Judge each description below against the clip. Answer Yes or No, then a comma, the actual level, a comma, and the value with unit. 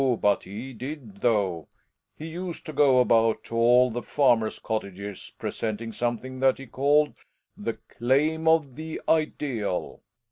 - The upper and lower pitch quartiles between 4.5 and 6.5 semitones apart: Yes, average, 4.8 semitones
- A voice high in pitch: No, low, 125 Hz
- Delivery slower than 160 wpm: Yes, average, 145 wpm